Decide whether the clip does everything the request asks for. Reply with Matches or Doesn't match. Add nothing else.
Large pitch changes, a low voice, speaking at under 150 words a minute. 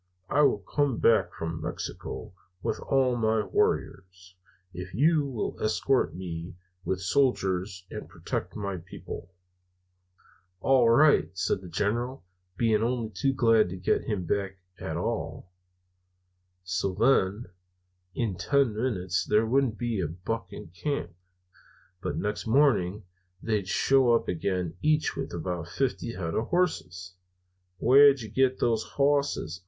Matches